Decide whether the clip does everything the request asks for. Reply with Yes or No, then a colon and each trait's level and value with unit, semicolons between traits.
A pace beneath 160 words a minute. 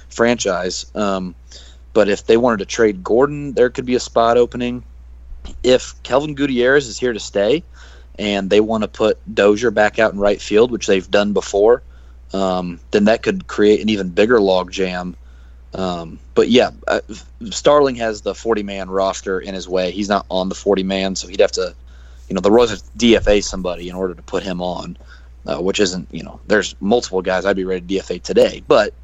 No: average, 200 wpm